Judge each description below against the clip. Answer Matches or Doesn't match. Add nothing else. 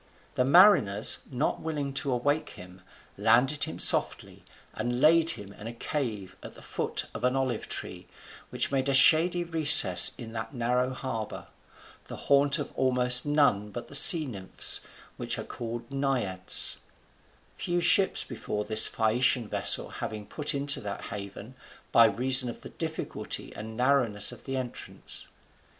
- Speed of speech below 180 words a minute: Matches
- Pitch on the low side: Matches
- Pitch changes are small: Doesn't match